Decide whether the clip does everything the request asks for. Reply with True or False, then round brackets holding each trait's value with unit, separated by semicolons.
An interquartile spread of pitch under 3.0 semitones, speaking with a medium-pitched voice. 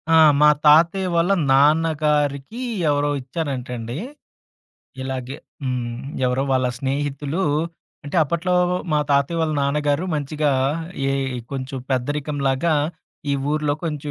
True (2.4 semitones; 145 Hz)